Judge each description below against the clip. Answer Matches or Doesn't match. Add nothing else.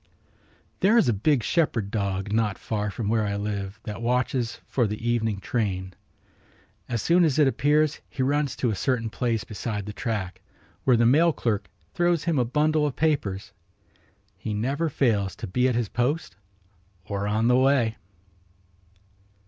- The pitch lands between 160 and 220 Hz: Doesn't match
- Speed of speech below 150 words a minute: Doesn't match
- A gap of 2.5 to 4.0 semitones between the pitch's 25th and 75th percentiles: Doesn't match